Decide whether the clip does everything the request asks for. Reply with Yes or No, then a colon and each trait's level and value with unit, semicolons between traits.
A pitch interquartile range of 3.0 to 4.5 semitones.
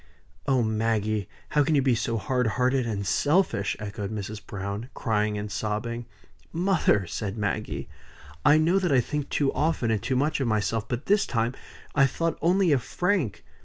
No: wide, 5.6 semitones